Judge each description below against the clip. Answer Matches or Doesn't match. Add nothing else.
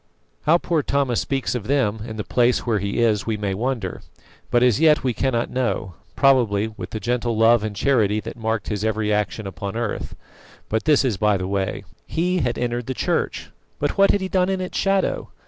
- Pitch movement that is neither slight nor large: Matches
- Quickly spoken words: Matches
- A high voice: Doesn't match